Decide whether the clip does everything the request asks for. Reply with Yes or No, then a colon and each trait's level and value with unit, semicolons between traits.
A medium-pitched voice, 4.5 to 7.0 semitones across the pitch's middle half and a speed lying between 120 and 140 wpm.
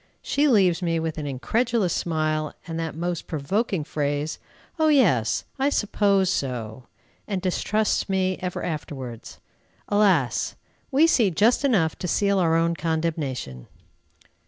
Yes: medium, 170 Hz; average, 5.0 semitones; slow, 135 wpm